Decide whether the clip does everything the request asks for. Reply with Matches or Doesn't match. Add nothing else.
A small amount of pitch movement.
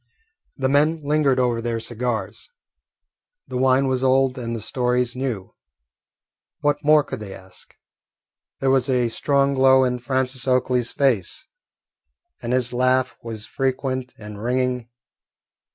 Matches